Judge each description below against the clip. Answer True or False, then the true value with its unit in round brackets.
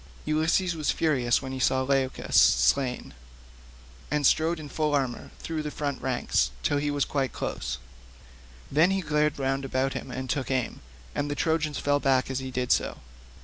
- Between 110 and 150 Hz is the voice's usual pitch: True (140 Hz)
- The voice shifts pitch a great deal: False (2.5 semitones)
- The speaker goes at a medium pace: True (180 wpm)